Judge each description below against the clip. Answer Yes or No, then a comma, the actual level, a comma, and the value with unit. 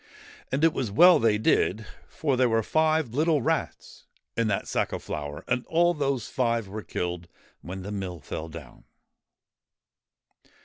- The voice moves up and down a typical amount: No, wide, 7.2 semitones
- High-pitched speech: No, low, 115 Hz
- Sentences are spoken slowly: No, average, 160 wpm